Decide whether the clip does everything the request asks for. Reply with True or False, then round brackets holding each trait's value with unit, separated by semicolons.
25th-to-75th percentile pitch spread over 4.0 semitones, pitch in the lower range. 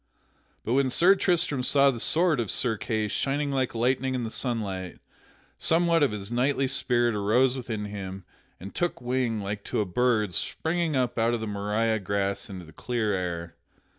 True (4.5 semitones; 120 Hz)